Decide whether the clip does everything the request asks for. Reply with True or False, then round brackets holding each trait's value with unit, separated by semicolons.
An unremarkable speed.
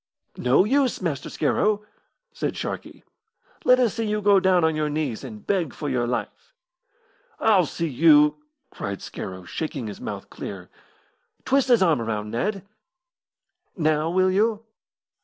True (150 wpm)